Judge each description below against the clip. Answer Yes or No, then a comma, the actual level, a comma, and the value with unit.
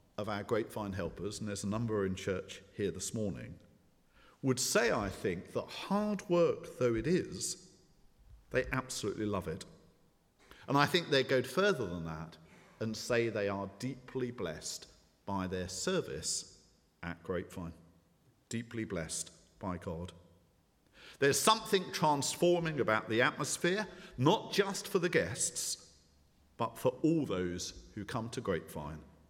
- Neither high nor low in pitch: No, low, 110 Hz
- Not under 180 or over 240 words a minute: No, average, 140 wpm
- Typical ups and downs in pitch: No, wide, 8.5 semitones